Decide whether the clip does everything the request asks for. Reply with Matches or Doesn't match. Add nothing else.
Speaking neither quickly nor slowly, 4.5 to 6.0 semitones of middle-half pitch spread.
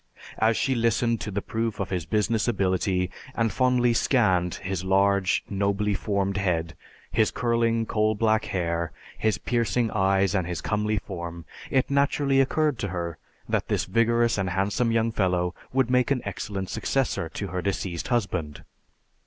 Doesn't match